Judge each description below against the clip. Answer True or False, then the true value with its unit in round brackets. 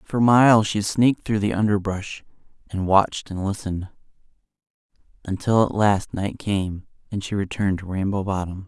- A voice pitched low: True (100 Hz)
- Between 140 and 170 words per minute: True (150 wpm)